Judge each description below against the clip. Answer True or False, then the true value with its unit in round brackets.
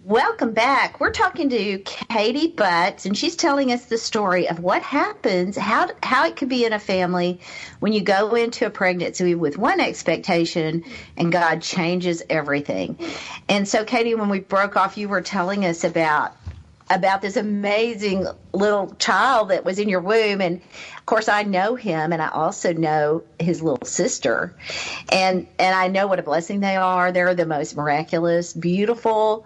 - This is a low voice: False (185 Hz)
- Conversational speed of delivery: True (175 wpm)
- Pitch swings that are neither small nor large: True (3.8 semitones)